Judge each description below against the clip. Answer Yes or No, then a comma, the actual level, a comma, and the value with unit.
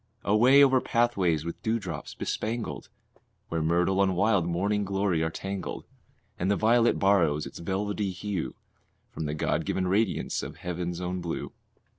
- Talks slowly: No, average, 150 wpm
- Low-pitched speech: Yes, very low, 95 Hz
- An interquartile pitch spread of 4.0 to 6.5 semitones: No, average, 3.4 semitones